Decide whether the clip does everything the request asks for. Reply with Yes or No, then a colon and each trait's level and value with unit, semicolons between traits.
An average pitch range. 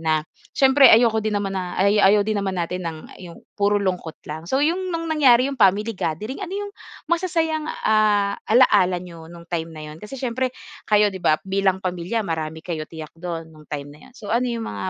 No: wide, 6.0 semitones